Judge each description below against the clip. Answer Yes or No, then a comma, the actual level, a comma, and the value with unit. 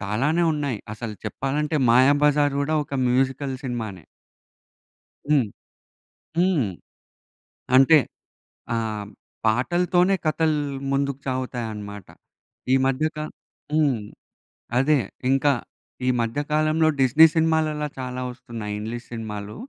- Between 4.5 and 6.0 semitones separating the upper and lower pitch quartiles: Yes, average, 4.8 semitones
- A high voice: No, low, 135 Hz